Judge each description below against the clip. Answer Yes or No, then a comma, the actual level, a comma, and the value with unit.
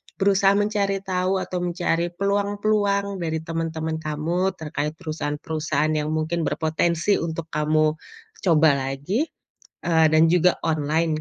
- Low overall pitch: No, medium, 165 Hz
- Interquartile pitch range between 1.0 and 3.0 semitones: No, average, 3.8 semitones